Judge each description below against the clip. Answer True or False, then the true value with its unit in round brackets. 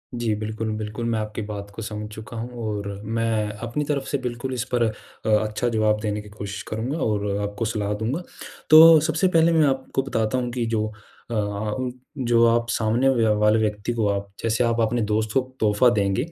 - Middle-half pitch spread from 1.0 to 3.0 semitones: True (2.4 semitones)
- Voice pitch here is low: True (110 Hz)